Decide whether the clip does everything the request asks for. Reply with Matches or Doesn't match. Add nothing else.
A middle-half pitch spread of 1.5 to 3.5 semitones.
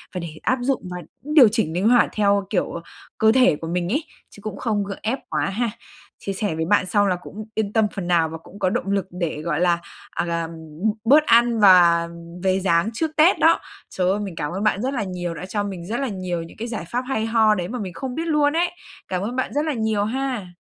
Doesn't match